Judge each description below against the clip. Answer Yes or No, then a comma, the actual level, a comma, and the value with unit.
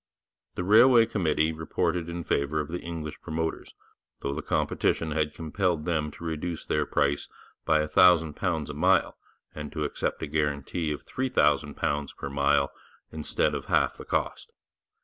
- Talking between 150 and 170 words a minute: Yes, average, 160 wpm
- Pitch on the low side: Yes, very low, 80 Hz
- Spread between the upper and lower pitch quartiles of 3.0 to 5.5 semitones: No, narrow, 2.5 semitones